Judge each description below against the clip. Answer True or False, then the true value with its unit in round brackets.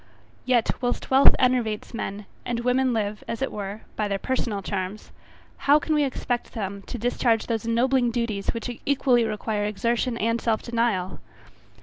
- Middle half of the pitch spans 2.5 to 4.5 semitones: True (2.9 semitones)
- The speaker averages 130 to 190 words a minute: True (160 wpm)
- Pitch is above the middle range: True (230 Hz)